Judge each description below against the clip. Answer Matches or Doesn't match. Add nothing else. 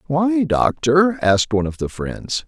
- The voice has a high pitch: Doesn't match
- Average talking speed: Matches